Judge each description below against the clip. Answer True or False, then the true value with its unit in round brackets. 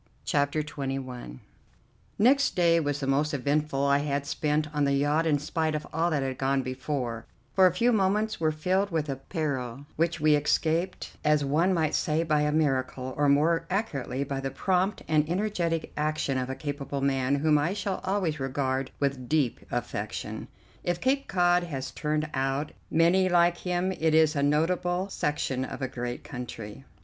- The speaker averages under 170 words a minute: False (180 wpm)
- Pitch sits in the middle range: True (150 Hz)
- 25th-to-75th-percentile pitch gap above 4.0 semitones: False (3.7 semitones)